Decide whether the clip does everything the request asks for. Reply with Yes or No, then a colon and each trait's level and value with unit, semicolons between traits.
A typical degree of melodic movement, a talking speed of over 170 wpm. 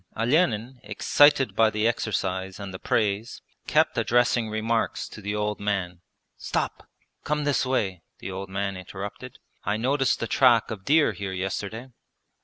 No: average, 3.8 semitones; average, 150 wpm